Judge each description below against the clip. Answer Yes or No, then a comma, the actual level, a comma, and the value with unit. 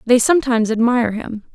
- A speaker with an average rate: Yes, average, 155 wpm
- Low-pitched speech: No, high, 235 Hz